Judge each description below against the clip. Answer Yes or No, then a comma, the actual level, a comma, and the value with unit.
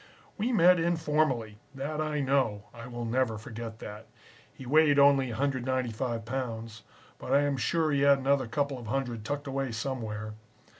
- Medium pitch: No, low, 130 Hz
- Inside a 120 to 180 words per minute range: Yes, average, 160 wpm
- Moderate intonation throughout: Yes, average, 3.7 semitones